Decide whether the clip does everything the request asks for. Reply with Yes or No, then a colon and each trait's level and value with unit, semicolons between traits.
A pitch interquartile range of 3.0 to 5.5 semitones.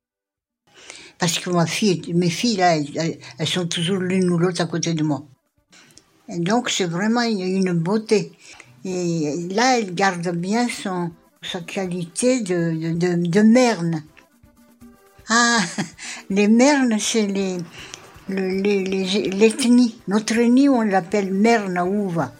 Yes: average, 4.1 semitones